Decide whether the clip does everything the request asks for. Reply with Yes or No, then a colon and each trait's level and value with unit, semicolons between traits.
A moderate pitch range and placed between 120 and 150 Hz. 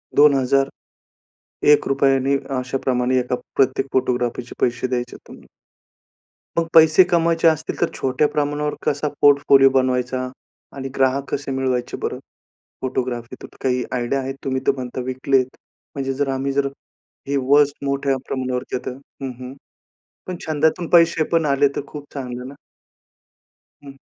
No: narrow, 2.0 semitones; low, 135 Hz